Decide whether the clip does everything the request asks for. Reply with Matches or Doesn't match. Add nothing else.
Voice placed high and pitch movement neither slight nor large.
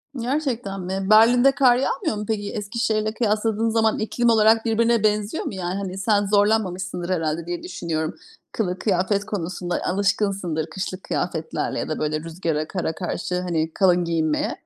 Matches